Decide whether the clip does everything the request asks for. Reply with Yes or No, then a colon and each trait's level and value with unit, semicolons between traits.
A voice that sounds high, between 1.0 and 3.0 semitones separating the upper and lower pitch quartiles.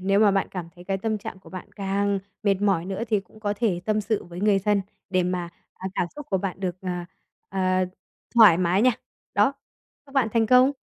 Yes: high, 195 Hz; narrow, 2.5 semitones